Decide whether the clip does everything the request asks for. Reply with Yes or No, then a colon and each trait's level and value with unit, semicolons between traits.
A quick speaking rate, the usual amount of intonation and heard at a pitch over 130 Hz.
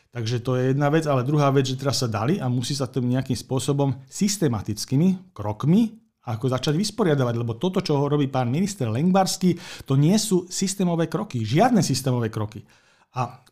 No: fast, 175 wpm; wide, 5.9 semitones; medium, 140 Hz